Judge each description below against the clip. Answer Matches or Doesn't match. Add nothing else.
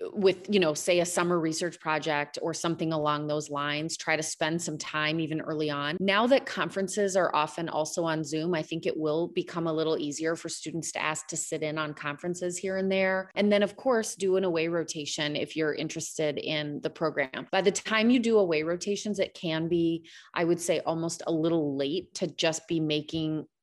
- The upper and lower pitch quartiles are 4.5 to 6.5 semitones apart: Doesn't match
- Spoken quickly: Matches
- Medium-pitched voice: Matches